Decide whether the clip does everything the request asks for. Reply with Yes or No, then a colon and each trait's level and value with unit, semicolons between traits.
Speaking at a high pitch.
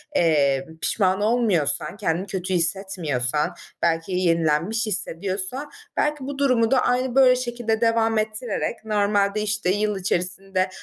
Yes: high, 200 Hz